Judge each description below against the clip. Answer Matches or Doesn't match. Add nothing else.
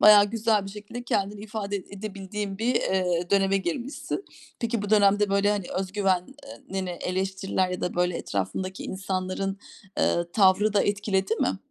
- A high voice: Matches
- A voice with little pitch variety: Matches